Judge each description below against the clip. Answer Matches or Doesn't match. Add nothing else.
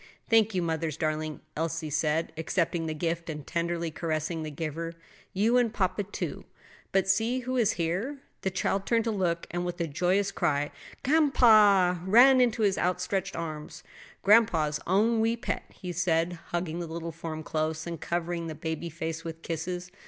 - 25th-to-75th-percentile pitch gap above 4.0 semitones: Doesn't match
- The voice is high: Doesn't match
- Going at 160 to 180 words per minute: Matches